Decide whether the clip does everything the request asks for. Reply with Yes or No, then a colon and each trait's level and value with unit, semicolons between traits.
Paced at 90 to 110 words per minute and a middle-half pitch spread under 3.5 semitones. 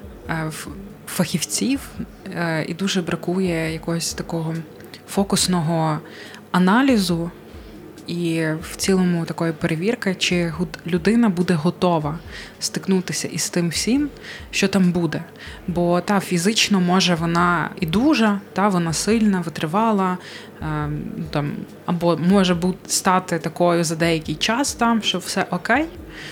Yes: slow, 105 wpm; average, 2.8 semitones